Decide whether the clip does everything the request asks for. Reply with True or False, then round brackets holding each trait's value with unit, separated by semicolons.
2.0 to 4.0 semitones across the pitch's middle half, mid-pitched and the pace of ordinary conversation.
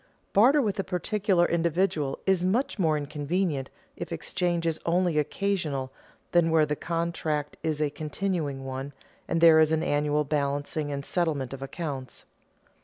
True (3.4 semitones; 160 Hz; 150 wpm)